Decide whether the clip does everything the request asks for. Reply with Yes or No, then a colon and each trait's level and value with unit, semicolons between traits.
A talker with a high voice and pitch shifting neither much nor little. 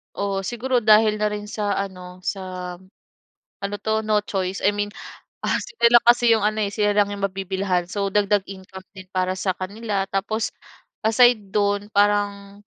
No: high, 205 Hz; narrow, 1.7 semitones